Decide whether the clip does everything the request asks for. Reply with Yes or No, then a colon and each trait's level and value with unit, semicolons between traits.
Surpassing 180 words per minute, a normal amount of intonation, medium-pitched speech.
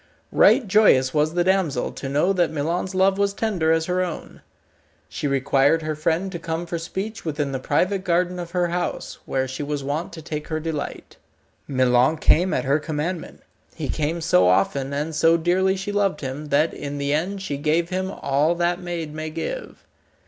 Yes: average, 190 wpm; average, 3.7 semitones; medium, 160 Hz